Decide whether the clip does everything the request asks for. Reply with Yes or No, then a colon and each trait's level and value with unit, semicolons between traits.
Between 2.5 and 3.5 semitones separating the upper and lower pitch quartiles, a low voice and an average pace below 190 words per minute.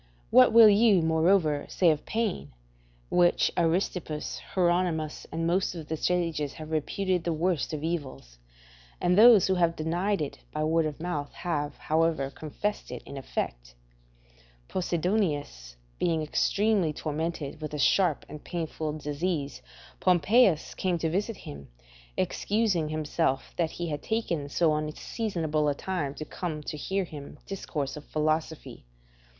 No: average, 3.2 semitones; medium, 160 Hz; average, 145 wpm